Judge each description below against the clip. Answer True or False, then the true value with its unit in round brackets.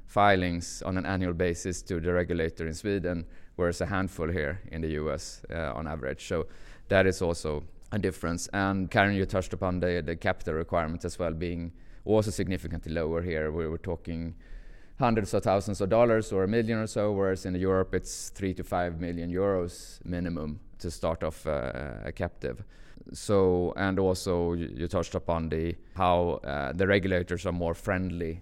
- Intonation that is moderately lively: False (2.2 semitones)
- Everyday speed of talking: True (175 wpm)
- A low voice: True (90 Hz)